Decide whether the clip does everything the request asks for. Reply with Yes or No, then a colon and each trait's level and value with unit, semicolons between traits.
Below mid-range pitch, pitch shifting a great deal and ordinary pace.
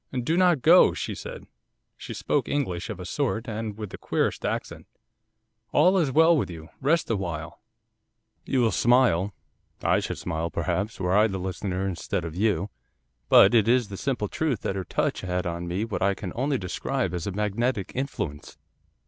Yes: low, 105 Hz; wide, 5.9 semitones; average, 180 wpm